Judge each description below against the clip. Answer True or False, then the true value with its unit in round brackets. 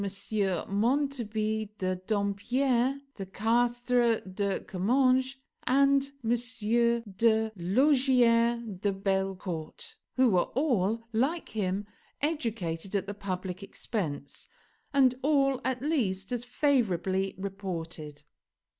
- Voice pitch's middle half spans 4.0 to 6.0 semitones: True (4.7 semitones)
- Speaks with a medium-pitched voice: False (220 Hz)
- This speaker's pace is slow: True (95 wpm)